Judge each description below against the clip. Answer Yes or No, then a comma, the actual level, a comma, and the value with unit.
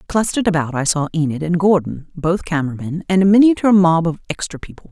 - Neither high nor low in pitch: Yes, medium, 175 Hz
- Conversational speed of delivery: No, fast, 210 wpm